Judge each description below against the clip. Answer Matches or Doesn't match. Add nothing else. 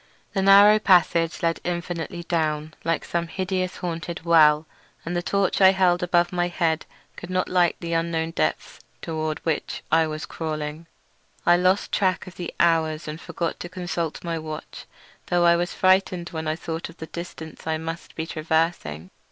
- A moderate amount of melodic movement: Doesn't match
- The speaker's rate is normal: Matches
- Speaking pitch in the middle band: Matches